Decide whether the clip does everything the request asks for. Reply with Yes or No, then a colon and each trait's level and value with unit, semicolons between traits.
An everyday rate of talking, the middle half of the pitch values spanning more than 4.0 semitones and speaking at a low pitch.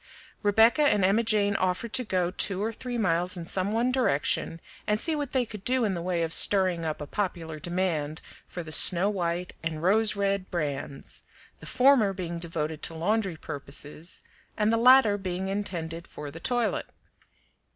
No: average, 180 wpm; average, 4.4 semitones; medium, 185 Hz